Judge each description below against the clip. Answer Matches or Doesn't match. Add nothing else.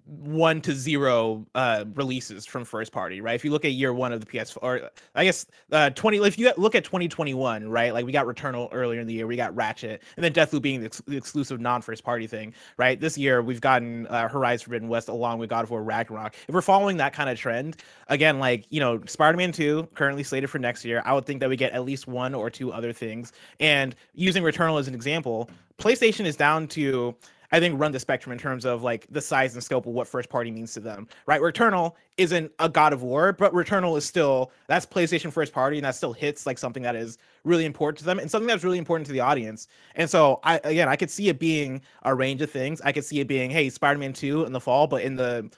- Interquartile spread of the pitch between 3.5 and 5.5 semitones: Matches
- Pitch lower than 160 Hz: Matches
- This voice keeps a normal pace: Doesn't match